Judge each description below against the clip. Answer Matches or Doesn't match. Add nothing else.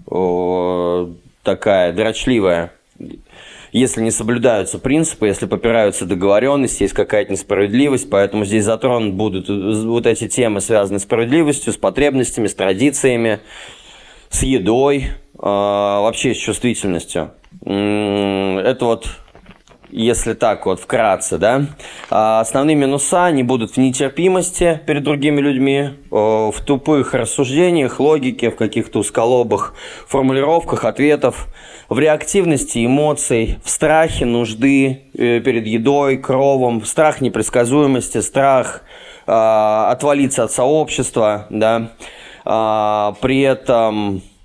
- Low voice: Matches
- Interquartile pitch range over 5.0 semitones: Doesn't match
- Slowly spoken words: Matches